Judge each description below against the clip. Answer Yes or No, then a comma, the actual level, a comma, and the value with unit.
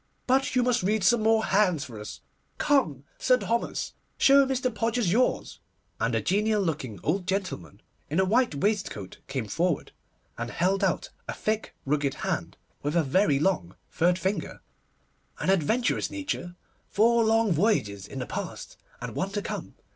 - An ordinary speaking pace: Yes, average, 160 wpm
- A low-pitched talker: No, high, 195 Hz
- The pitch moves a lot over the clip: Yes, wide, 6.9 semitones